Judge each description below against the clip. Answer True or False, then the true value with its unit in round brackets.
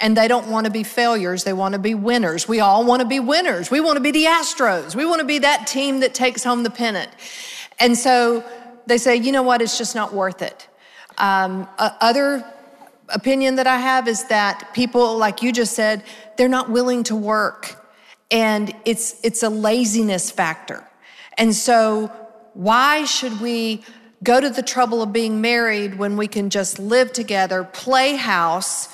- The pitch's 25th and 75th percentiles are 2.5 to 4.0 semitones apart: True (2.9 semitones)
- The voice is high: True (230 Hz)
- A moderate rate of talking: True (190 wpm)